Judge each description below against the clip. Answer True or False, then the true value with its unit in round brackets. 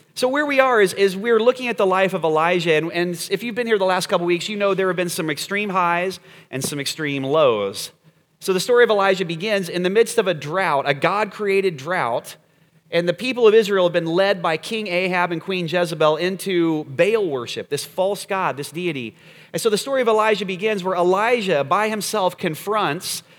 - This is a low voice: False (185 Hz)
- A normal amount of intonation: True (3.7 semitones)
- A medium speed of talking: False (220 wpm)